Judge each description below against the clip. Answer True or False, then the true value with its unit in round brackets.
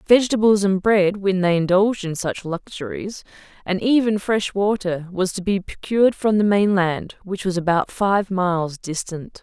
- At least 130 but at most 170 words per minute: True (165 wpm)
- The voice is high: True (195 Hz)